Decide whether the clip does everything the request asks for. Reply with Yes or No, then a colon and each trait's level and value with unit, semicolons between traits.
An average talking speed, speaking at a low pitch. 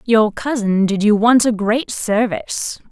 No: average, 165 wpm; high, 220 Hz